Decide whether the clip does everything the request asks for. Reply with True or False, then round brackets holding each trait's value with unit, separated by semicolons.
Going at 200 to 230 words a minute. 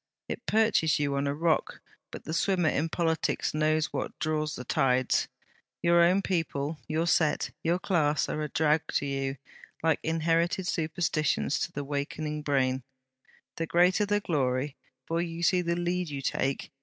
False (165 wpm)